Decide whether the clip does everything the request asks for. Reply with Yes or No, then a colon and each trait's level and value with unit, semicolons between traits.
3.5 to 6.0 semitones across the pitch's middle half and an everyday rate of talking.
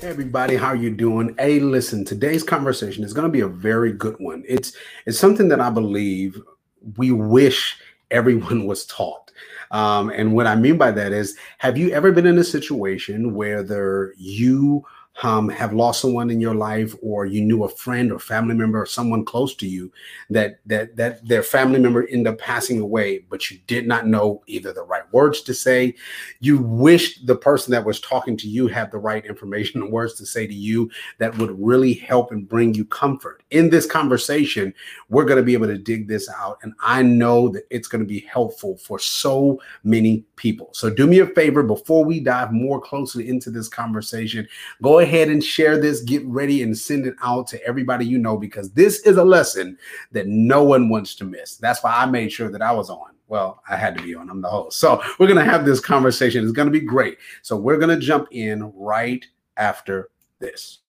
No: average, 3.9 semitones; fast, 215 wpm